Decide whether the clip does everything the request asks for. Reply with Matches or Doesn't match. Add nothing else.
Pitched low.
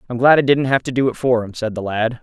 Matches